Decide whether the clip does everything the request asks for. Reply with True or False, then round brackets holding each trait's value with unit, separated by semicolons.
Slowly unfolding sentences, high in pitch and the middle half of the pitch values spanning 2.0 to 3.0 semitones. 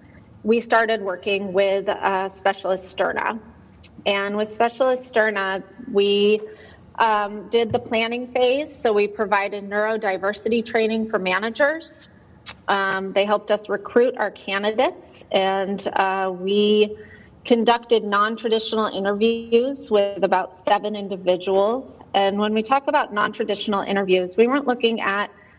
True (125 wpm; 210 Hz; 2.7 semitones)